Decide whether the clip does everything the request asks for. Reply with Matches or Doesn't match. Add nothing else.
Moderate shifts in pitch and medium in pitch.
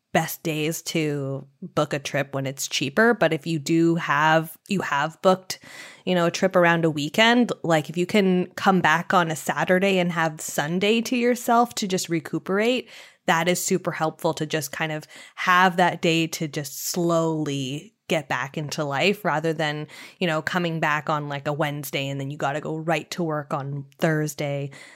Matches